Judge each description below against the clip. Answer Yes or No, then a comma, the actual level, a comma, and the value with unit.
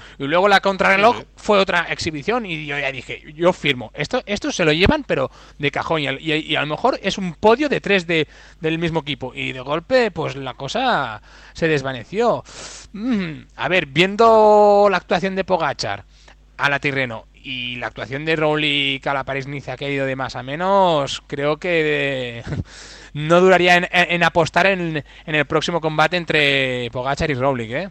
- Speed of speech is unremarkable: No, fast, 195 wpm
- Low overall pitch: No, medium, 155 Hz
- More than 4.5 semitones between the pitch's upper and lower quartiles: Yes, average, 5.0 semitones